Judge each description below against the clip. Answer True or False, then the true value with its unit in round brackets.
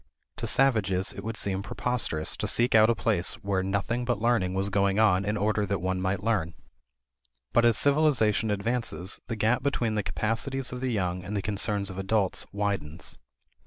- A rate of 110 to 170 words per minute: False (185 wpm)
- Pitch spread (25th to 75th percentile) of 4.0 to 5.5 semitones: False (3.4 semitones)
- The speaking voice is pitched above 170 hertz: False (105 Hz)